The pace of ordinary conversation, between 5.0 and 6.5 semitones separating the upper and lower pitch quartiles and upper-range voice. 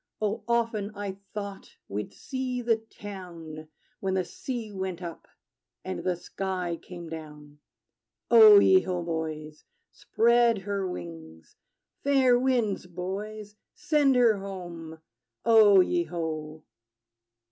No: slow, 115 wpm; wide, 5.6 semitones; high, 195 Hz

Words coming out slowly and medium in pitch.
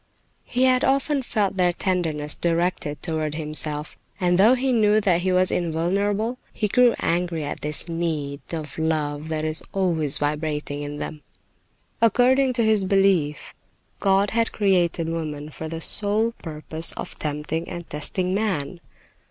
No: average, 150 wpm; medium, 170 Hz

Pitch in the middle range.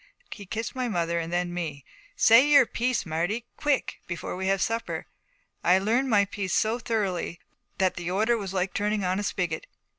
No: high, 195 Hz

